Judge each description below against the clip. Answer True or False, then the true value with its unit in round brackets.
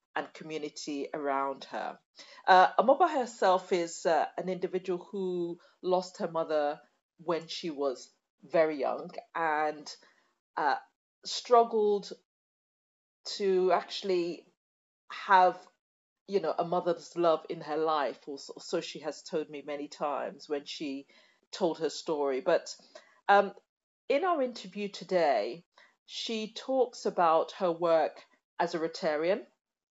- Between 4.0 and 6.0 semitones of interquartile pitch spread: True (4.3 semitones)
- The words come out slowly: True (120 wpm)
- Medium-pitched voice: True (175 Hz)